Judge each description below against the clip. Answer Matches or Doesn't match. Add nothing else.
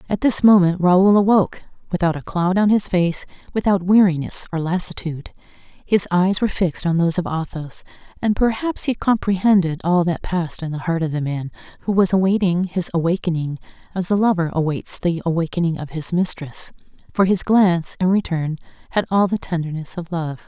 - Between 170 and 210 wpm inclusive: Matches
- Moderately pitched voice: Matches